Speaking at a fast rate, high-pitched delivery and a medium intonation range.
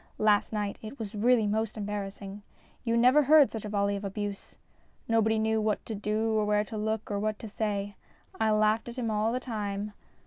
No: fast, 210 wpm; high, 215 Hz; narrow, 1.4 semitones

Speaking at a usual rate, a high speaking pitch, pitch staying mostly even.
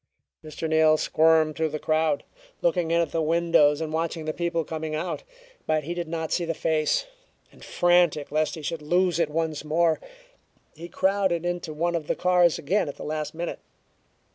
No: average, 190 wpm; medium, 160 Hz; narrow, 1.7 semitones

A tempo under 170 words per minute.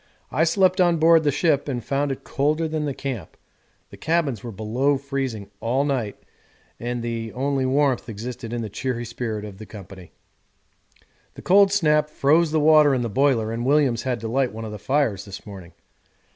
No: average, 190 wpm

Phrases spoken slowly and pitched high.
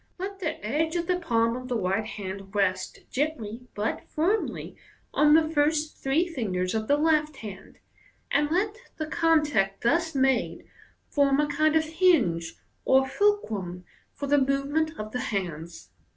No: average, 160 wpm; very high, 275 Hz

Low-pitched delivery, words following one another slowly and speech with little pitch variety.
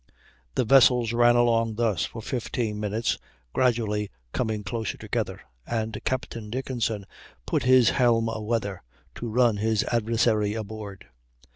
Yes: low, 115 Hz; slow, 125 wpm; narrow, 2.1 semitones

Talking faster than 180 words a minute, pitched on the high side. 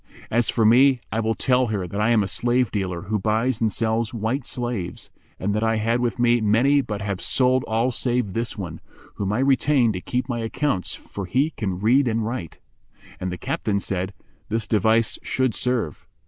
No: average, 200 wpm; low, 115 Hz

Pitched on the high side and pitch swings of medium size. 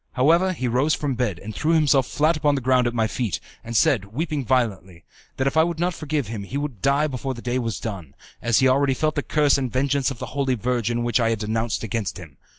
No: low, 130 Hz; average, 4.1 semitones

